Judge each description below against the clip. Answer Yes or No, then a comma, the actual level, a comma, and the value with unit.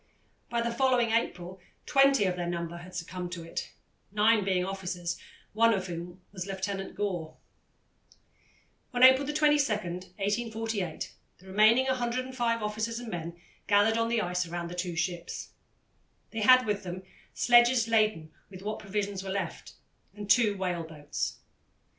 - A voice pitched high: Yes, high, 200 Hz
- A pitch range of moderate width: Yes, average, 4.3 semitones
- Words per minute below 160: Yes, average, 145 wpm